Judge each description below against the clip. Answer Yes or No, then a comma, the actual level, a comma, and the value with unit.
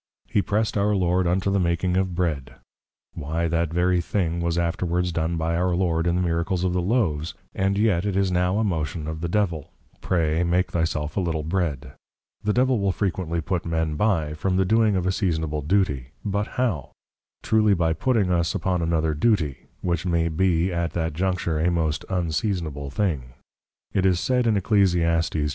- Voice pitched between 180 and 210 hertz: No, very low, 85 Hz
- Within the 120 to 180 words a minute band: No, average, 190 wpm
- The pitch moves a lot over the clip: No, average, 2.8 semitones